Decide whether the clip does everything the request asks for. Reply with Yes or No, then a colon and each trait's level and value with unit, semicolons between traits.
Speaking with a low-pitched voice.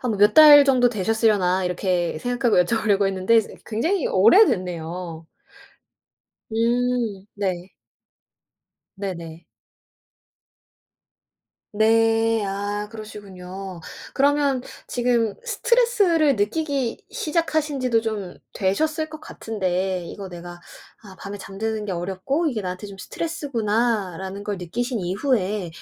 No: high, 215 Hz